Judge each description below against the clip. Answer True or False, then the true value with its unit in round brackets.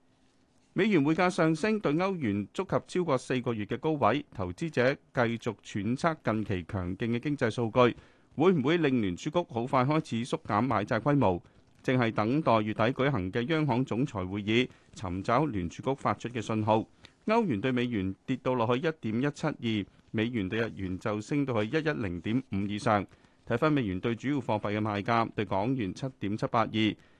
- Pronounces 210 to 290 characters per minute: True (280 characters per minute)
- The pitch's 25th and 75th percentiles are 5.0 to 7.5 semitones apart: False (4.6 semitones)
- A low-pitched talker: True (120 Hz)